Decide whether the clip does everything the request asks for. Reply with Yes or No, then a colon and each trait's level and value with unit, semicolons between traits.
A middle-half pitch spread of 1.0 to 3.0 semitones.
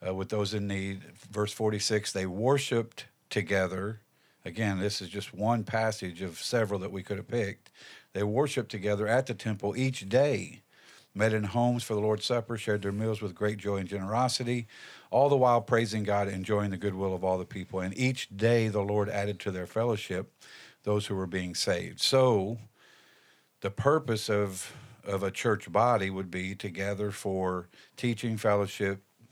Yes: average, 2.7 semitones